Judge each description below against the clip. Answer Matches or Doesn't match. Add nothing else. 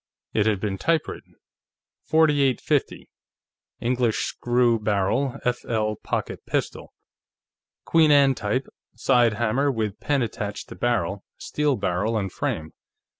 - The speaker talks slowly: Matches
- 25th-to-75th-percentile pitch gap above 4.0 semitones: Matches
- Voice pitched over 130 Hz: Doesn't match